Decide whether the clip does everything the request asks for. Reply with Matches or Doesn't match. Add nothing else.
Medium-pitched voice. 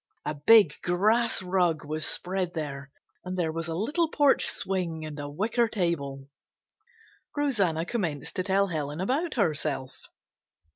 Matches